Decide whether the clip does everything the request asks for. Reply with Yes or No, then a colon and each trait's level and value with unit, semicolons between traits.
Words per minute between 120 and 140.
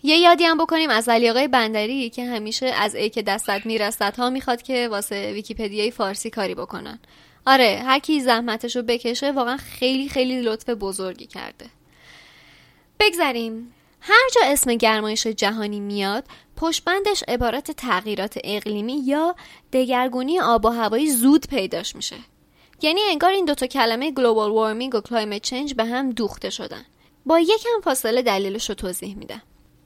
No: average, 150 wpm